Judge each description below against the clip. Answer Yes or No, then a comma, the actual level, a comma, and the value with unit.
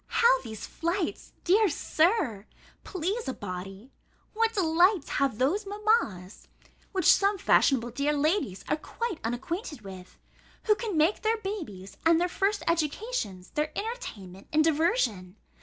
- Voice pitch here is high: Yes, very high, 320 Hz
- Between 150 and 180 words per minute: No, slow, 135 wpm